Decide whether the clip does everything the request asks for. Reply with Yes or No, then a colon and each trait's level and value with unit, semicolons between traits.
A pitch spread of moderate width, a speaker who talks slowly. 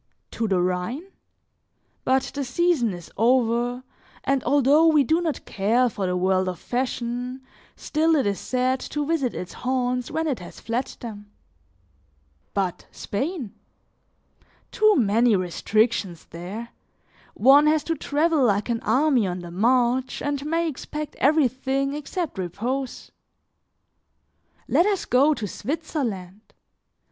No: wide, 5.8 semitones; slow, 130 wpm